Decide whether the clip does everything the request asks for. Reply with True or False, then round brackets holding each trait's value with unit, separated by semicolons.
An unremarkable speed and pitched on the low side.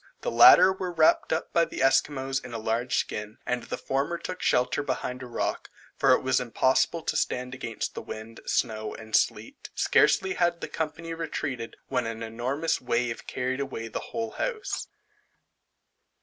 True (170 wpm; 130 Hz)